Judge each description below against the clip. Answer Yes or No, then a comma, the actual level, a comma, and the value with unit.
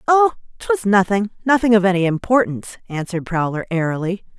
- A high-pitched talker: Yes, high, 205 Hz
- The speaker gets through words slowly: Yes, slow, 125 wpm